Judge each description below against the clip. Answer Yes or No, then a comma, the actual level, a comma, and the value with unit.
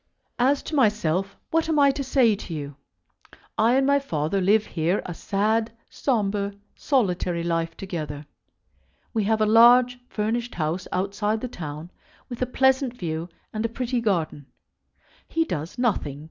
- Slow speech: No, average, 155 wpm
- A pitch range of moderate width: No, wide, 6.2 semitones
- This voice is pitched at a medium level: No, high, 210 Hz